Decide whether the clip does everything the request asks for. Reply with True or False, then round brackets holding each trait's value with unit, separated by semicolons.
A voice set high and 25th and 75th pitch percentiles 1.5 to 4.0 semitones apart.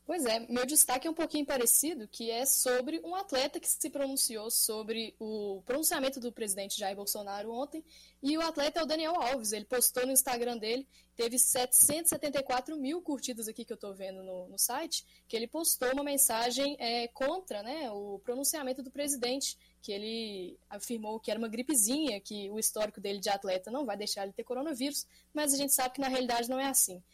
False (250 Hz; 4.4 semitones)